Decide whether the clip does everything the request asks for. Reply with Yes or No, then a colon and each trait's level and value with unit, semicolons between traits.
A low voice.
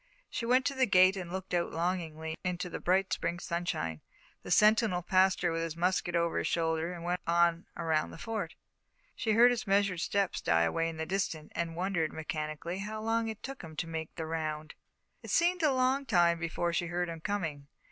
No: medium, 175 Hz